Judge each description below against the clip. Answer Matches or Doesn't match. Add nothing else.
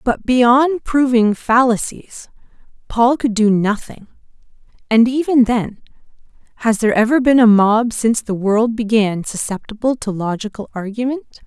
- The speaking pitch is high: Matches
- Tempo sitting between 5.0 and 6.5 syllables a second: Doesn't match